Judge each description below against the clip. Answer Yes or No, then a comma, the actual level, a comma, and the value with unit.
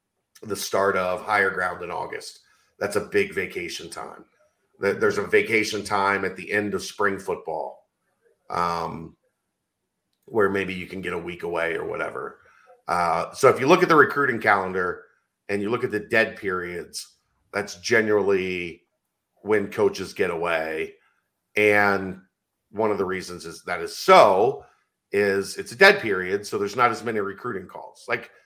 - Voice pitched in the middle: No, low, 115 Hz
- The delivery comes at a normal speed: Yes, average, 160 wpm